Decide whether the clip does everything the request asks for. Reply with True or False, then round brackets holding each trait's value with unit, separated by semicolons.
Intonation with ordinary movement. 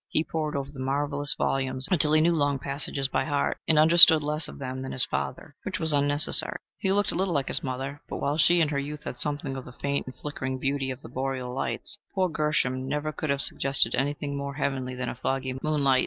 False (2.3 semitones)